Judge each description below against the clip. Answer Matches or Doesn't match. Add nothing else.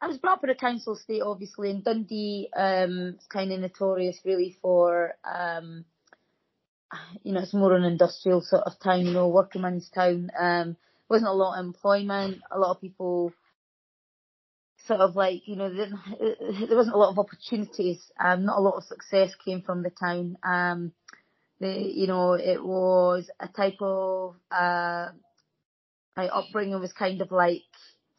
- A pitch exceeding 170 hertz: Matches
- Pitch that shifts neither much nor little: Doesn't match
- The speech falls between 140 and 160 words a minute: Doesn't match